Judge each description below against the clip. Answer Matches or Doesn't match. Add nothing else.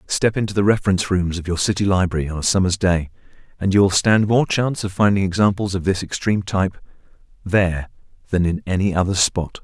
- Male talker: Matches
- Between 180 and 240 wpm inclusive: Matches